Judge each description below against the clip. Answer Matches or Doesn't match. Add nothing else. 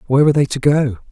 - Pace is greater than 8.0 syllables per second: Matches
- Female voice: Doesn't match